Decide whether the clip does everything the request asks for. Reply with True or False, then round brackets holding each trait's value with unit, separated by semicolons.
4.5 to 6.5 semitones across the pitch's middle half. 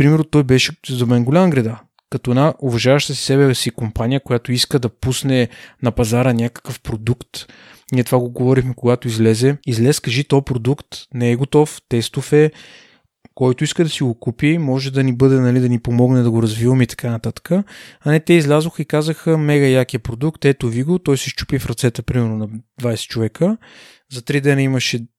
False (2.9 semitones)